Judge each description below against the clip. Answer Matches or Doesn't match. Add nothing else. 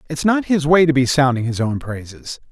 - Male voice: Matches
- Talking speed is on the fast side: Matches